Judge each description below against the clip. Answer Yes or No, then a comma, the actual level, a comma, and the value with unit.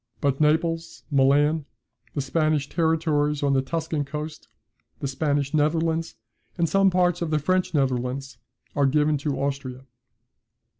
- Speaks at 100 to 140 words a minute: Yes, slow, 135 wpm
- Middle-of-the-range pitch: Yes, medium, 150 Hz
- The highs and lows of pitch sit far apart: No, average, 2.7 semitones